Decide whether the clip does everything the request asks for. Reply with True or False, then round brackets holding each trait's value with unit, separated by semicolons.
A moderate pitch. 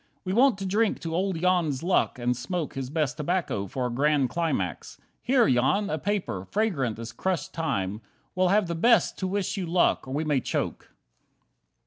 True (165 Hz)